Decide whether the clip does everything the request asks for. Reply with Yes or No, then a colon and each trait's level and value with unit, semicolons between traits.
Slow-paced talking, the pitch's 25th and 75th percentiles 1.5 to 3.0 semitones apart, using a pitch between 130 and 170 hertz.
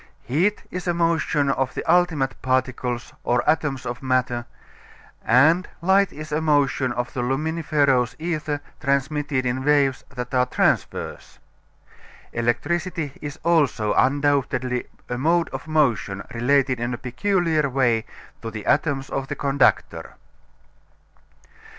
No: slow, 125 wpm; average, 3.8 semitones; medium, 140 Hz